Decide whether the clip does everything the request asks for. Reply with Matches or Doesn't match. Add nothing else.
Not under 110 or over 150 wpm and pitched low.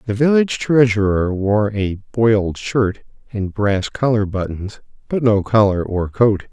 Matches